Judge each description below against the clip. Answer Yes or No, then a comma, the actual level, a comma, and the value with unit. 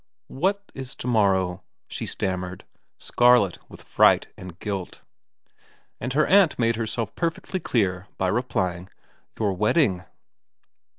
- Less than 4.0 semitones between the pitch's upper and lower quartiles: No, wide, 5.4 semitones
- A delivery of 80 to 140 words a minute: Yes, slow, 135 wpm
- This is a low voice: Yes, low, 105 Hz